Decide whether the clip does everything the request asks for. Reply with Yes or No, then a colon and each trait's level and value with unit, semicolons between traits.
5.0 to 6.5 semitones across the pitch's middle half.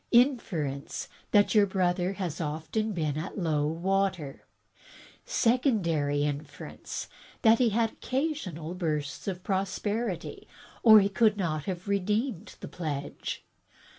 Yes: wide, 5.6 semitones